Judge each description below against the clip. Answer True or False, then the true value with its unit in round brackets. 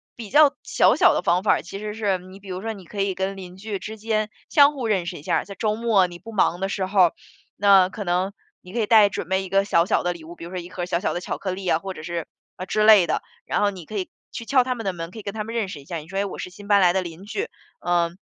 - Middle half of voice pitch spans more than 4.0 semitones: False (3.0 semitones)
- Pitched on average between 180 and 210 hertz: True (195 Hz)